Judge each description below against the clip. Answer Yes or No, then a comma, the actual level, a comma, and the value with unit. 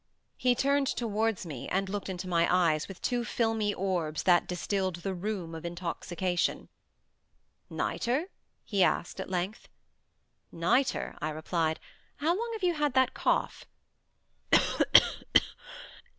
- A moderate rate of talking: No, slow, 125 wpm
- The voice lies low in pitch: No, high, 190 Hz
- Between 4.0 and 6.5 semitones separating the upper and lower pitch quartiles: Yes, wide, 5.5 semitones